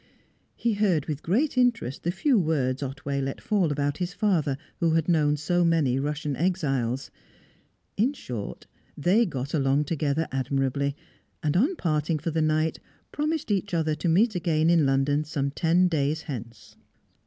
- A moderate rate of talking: Yes, average, 160 wpm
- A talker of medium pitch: Yes, medium, 155 Hz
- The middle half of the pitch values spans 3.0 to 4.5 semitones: Yes, average, 4.2 semitones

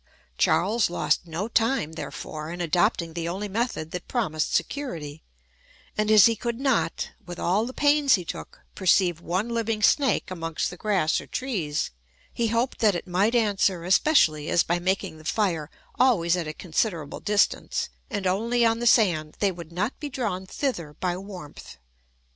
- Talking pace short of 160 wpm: No, average, 170 wpm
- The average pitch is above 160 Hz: Yes, high, 190 Hz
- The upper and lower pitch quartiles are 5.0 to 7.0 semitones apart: Yes, average, 5.3 semitones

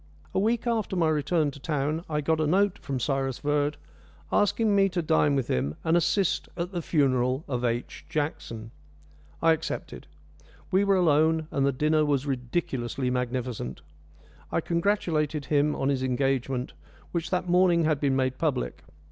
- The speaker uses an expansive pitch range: No, average, 4.3 semitones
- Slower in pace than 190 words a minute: Yes, average, 165 wpm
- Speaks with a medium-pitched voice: Yes, medium, 150 Hz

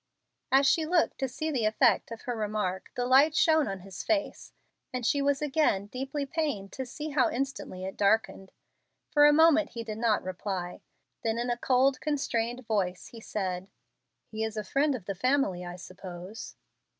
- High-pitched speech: Yes, high, 240 Hz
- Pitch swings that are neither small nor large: No, wide, 6.1 semitones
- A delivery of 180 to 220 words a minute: Yes, average, 185 wpm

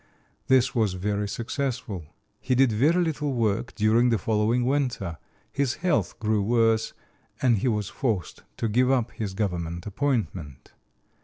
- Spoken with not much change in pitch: No, average, 3.9 semitones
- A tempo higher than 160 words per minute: No, average, 145 wpm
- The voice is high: No, low, 115 Hz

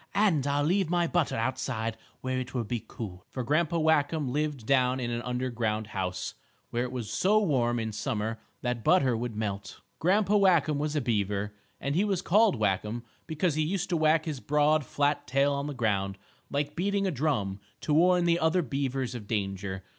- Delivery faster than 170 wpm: Yes, average, 190 wpm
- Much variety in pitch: Yes, wide, 5.9 semitones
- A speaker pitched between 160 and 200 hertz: No, low, 135 Hz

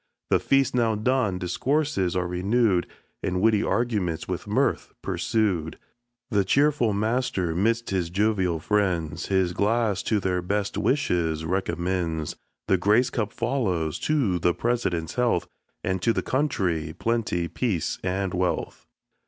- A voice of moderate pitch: No, low, 100 Hz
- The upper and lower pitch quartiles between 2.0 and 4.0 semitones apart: No, average, 4.7 semitones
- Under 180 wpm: Yes, slow, 135 wpm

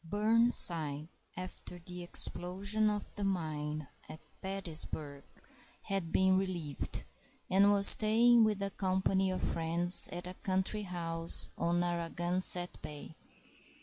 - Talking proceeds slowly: Yes, slow, 115 wpm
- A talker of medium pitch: Yes, medium, 180 Hz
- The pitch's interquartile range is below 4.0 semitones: Yes, average, 2.9 semitones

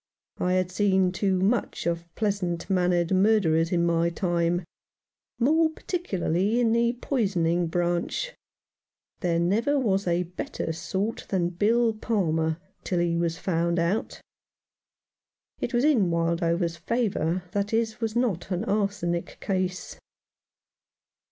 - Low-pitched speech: No, medium, 185 Hz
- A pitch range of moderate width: Yes, average, 4.1 semitones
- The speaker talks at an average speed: No, slow, 125 wpm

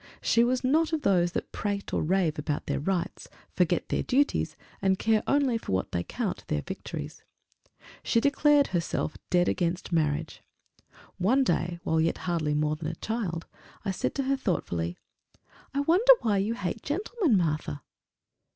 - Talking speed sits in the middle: Yes, average, 165 wpm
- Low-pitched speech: No, high, 190 Hz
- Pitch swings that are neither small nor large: No, wide, 8.2 semitones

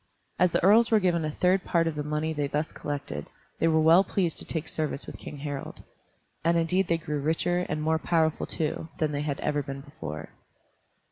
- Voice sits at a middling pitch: Yes, medium, 160 Hz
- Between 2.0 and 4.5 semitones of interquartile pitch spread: Yes, narrow, 2.4 semitones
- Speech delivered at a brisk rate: Yes, fast, 210 wpm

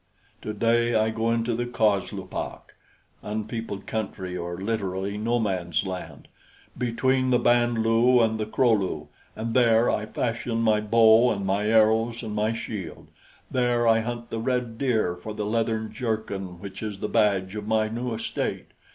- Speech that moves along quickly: No, average, 160 wpm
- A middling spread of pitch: No, narrow, 2.0 semitones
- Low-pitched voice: Yes, low, 110 Hz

